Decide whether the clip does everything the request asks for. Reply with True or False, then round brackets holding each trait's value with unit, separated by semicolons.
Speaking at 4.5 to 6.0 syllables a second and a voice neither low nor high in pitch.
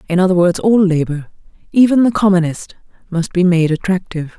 True (5.9 syllables/s; 180 Hz)